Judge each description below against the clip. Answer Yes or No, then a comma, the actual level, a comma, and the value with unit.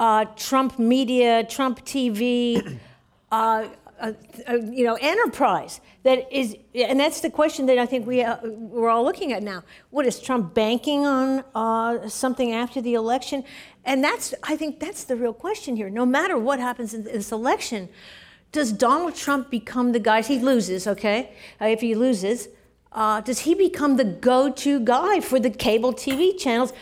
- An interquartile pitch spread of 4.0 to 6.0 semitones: No, average, 2.9 semitones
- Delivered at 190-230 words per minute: No, average, 175 wpm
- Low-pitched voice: No, very high, 250 Hz